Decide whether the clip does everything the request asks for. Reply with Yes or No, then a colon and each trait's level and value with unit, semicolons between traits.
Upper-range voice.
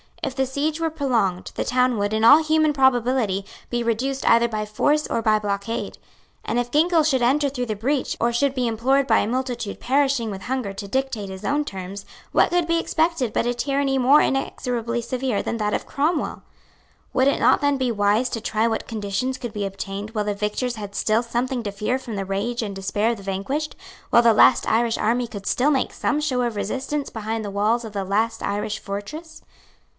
Yes: high, 235 Hz